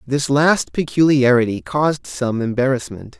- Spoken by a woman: No, male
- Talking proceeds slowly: Yes, slow, 115 wpm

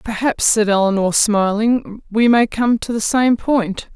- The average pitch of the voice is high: Yes, high, 220 Hz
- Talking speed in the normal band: Yes, average, 165 wpm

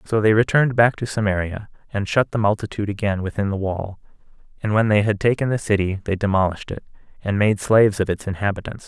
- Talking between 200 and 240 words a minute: Yes, fast, 205 wpm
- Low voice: Yes, low, 105 Hz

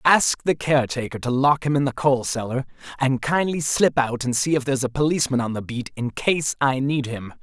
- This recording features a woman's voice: No, male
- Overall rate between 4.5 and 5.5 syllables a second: Yes, 5.4 syllables/s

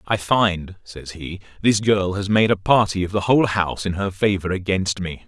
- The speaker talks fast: Yes, fast, 215 wpm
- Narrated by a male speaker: Yes, male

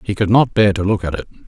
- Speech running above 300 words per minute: Yes, fast, 325 wpm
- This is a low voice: Yes, low, 100 Hz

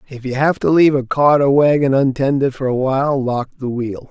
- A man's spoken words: Yes, male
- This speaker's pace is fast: Yes, fast, 235 wpm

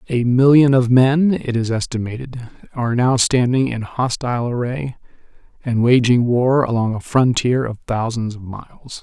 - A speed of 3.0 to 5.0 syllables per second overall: Yes, 4.7 syllables/s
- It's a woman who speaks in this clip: No, male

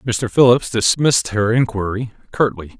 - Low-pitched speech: Yes, low, 115 Hz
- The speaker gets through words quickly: No, slow, 130 wpm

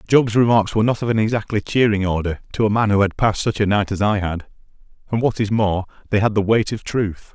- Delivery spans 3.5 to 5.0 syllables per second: No, 6.1 syllables/s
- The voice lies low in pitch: Yes, low, 105 Hz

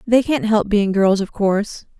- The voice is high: Yes, high, 210 Hz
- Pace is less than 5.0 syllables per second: Yes, 4.6 syllables/s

